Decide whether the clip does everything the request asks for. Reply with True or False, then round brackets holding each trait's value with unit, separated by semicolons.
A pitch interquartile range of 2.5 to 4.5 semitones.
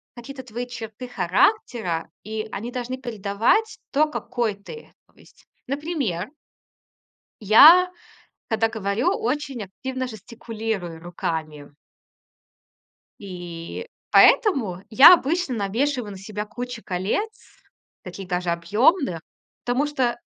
False (5.3 semitones)